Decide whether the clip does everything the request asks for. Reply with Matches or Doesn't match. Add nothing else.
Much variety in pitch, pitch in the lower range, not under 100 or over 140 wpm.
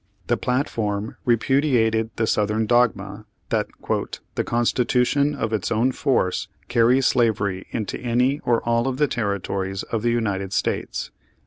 Doesn't match